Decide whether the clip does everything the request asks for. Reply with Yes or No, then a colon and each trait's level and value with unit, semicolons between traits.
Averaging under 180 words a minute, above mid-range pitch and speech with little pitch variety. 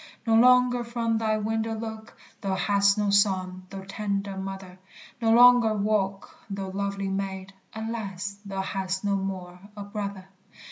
Yes: average, 145 wpm; high, 200 Hz; narrow, 2.3 semitones